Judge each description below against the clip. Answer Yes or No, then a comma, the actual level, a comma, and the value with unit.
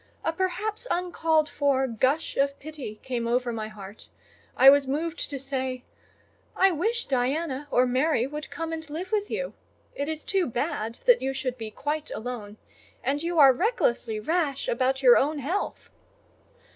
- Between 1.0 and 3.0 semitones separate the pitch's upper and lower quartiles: No, average, 4.4 semitones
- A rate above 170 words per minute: No, average, 165 wpm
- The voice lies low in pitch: No, very high, 280 Hz